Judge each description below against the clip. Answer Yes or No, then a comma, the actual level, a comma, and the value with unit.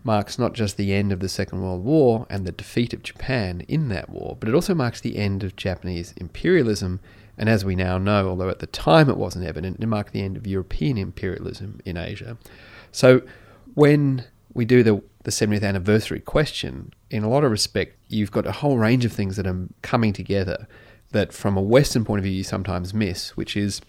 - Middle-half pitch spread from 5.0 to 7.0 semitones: No, average, 3.5 semitones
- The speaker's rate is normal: No, fast, 215 wpm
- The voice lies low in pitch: Yes, low, 105 Hz